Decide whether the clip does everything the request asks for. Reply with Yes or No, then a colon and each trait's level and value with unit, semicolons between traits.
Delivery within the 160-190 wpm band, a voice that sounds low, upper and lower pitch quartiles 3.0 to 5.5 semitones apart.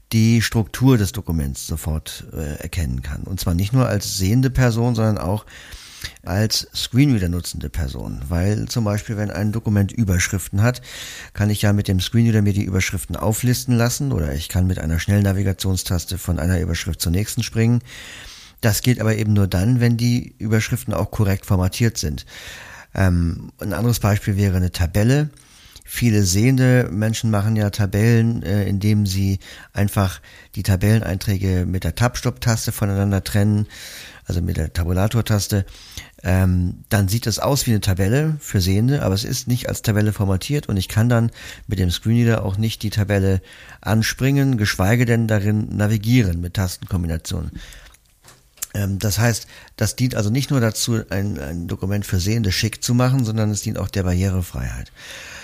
Yes: average, 165 wpm; low, 105 Hz; average, 3.5 semitones